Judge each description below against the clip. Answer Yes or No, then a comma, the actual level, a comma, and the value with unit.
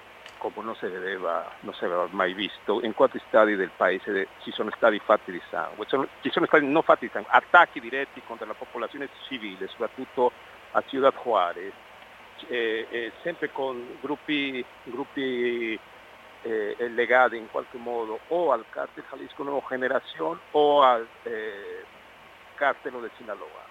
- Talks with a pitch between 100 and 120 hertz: No, low, 130 Hz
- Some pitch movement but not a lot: Yes, average, 4.3 semitones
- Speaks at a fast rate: No, average, 145 wpm